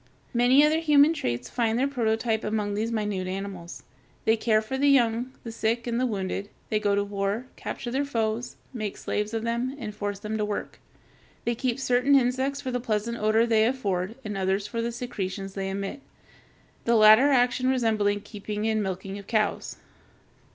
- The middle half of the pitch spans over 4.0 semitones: No, average, 3.2 semitones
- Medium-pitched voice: No, high, 220 Hz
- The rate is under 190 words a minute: Yes, average, 180 wpm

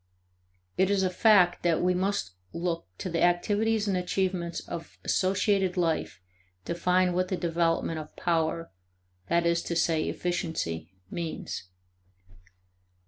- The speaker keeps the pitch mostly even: Yes, narrow, 1.9 semitones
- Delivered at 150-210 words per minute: No, slow, 135 wpm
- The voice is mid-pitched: Yes, medium, 175 Hz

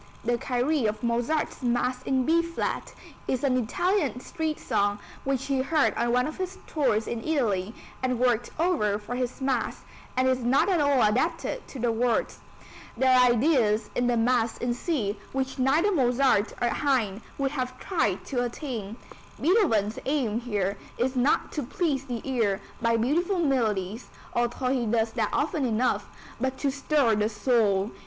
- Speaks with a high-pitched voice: Yes, very high, 250 Hz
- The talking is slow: No, average, 170 wpm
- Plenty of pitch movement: No, average, 3.5 semitones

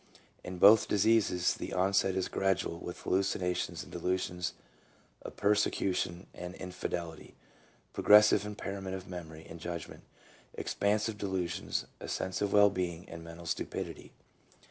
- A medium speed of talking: No, slow, 130 wpm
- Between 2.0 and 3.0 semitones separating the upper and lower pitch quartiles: Yes, narrow, 2.4 semitones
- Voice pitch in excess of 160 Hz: No, very low, 95 Hz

